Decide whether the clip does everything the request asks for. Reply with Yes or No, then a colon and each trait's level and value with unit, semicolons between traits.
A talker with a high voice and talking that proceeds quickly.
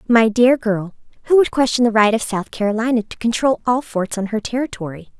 Yes: high, 230 Hz; fast, 210 wpm